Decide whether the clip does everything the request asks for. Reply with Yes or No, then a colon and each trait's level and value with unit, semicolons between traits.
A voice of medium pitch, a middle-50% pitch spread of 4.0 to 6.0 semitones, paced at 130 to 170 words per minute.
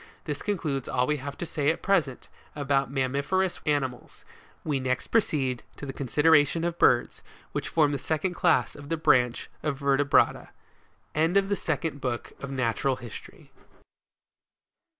No: medium, 145 Hz; average, 3.4 semitones; average, 150 wpm